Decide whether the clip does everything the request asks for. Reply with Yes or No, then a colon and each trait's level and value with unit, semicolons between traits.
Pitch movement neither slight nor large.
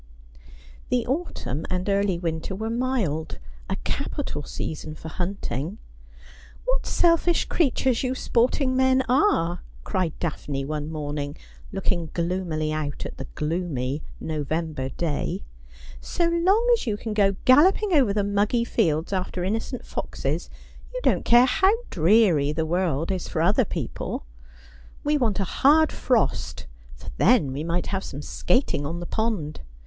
No: wide, 8.0 semitones